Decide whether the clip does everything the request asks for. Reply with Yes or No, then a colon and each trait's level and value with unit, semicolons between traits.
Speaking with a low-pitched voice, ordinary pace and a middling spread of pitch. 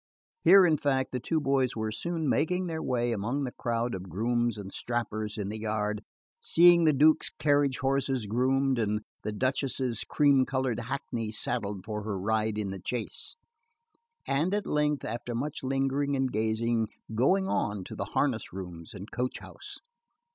Yes: low, 120 Hz; average, 170 wpm; average, 4.4 semitones